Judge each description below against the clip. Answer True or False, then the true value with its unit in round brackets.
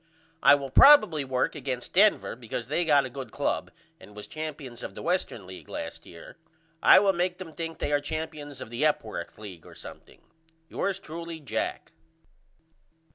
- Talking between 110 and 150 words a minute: False (175 wpm)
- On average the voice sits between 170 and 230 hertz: False (145 Hz)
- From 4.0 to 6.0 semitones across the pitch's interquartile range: True (5.1 semitones)